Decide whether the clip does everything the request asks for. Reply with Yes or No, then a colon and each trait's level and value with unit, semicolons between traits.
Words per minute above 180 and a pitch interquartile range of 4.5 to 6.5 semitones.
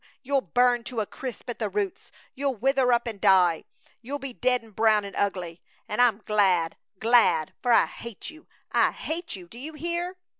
Yes: average, 195 wpm; average, 4.9 semitones